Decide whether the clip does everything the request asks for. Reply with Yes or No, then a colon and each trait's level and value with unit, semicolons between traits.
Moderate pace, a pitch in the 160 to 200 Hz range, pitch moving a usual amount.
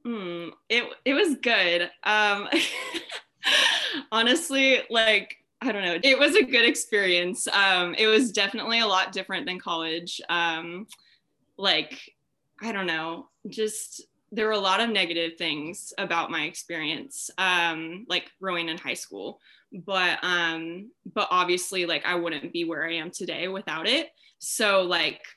Yes: average, 150 wpm; high, 190 Hz; average, 4.7 semitones